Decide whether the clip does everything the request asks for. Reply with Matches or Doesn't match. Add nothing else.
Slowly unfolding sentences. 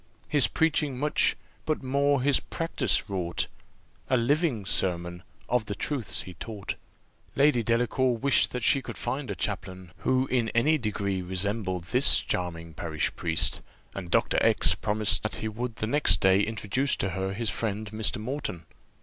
Doesn't match